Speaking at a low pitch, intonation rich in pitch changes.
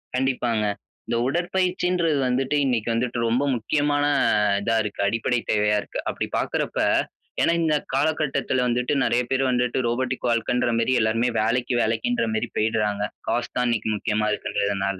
No: low, 125 Hz; average, 3.4 semitones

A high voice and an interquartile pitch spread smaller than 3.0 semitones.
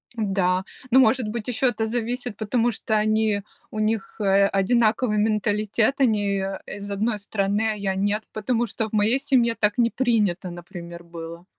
Yes: high, 215 Hz; narrow, 2.6 semitones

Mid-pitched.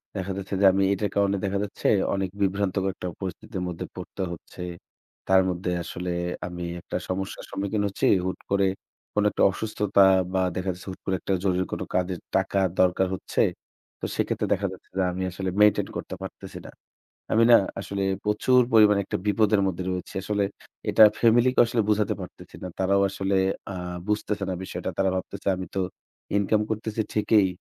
No: low, 100 Hz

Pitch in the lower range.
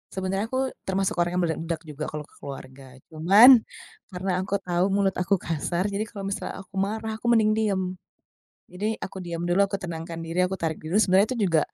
No: medium, 185 Hz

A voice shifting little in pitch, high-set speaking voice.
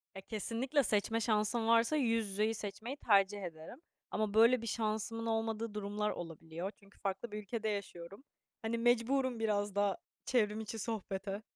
Yes: narrow, 2.3 semitones; high, 215 Hz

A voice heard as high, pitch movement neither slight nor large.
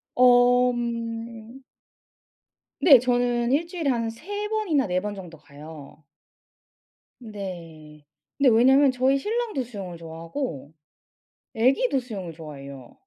No: high, 235 Hz; wide, 7.7 semitones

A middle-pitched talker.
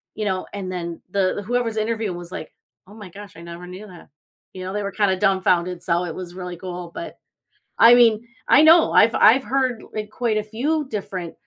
No: high, 200 Hz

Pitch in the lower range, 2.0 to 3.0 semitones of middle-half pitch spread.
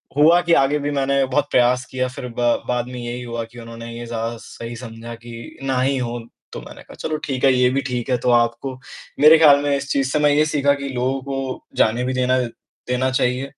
Yes: low, 130 Hz; narrow, 2.5 semitones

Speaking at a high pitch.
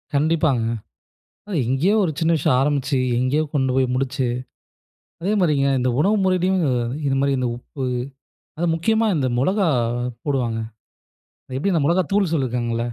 No: medium, 145 Hz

